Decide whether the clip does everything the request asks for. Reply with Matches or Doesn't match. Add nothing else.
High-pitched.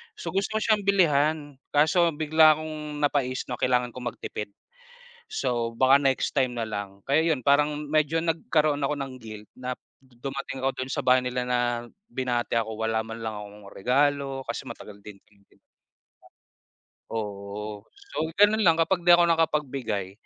Doesn't match